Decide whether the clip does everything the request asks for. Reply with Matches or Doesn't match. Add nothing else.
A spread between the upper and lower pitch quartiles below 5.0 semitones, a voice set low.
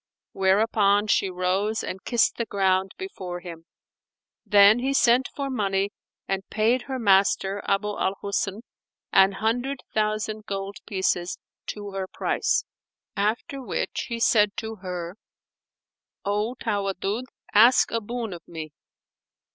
Doesn't match